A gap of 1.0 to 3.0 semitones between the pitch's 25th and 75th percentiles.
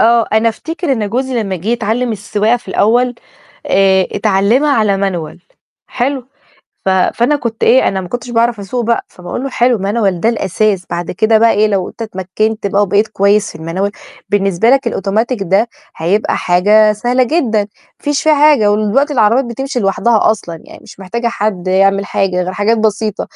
No: average, 3.5 semitones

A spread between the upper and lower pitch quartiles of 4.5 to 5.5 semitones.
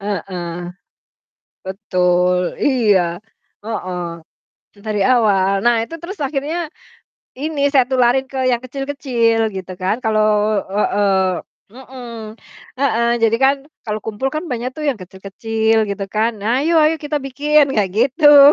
Yes: average, 5.2 semitones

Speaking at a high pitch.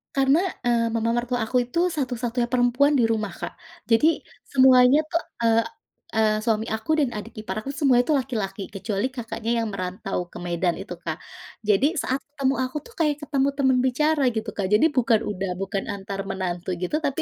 Yes: high, 235 Hz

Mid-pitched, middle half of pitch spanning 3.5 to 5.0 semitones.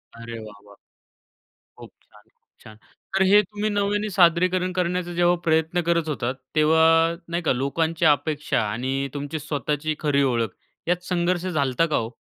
Yes: medium, 160 Hz; average, 4.2 semitones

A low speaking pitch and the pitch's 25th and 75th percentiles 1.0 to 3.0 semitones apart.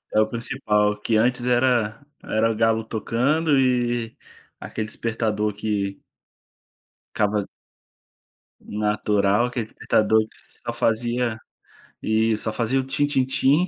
Yes: low, 115 Hz; narrow, 2.5 semitones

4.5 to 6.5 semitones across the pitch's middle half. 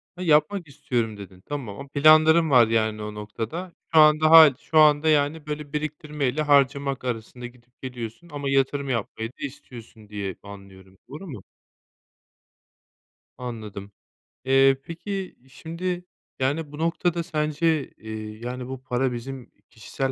Yes: average, 5.1 semitones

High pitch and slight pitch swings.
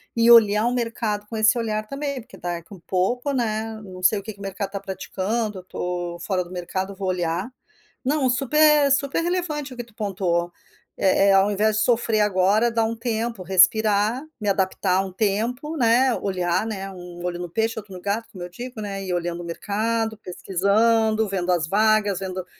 No: high, 210 Hz; average, 3.6 semitones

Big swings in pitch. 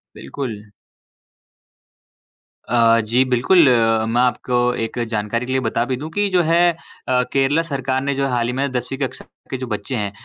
No: average, 2.7 semitones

